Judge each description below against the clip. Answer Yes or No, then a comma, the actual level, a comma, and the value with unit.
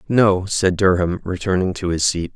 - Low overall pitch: Yes, very low, 90 Hz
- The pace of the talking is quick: No, average, 180 wpm